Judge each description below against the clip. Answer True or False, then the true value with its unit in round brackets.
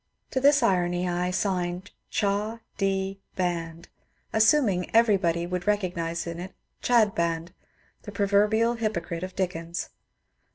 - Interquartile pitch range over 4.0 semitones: False (3.2 semitones)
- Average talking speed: False (120 wpm)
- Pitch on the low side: False (185 Hz)